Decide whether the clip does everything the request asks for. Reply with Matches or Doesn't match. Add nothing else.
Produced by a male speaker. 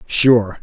Matches